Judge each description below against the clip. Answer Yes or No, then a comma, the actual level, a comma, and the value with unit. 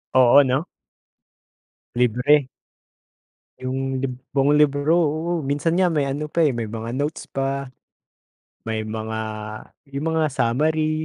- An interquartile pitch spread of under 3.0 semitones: No, average, 3.3 semitones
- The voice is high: No, medium, 140 Hz